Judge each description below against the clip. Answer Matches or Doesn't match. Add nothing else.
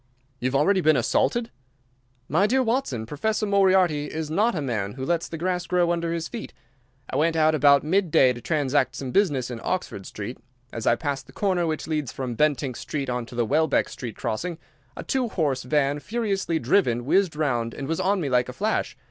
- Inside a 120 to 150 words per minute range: Doesn't match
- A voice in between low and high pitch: Matches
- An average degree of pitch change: Doesn't match